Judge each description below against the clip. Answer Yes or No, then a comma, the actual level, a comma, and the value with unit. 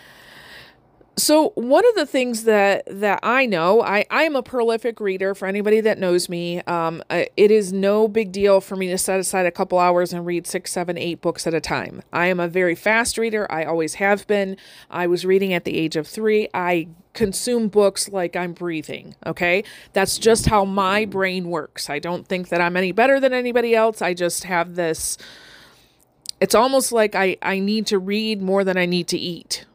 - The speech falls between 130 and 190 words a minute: No, fast, 205 wpm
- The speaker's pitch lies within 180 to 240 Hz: Yes, high, 190 Hz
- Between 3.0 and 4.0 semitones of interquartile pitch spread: Yes, average, 3.4 semitones